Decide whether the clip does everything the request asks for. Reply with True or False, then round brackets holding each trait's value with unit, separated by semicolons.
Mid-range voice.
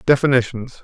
False (125 Hz)